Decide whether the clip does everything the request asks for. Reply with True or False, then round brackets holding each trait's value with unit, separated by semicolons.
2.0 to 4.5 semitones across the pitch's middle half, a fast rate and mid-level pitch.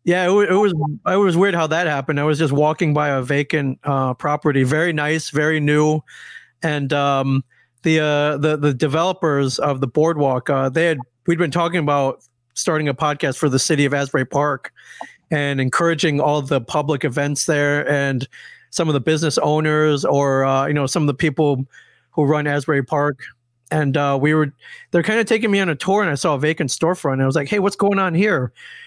True (2.7 semitones; 210 wpm; 150 Hz)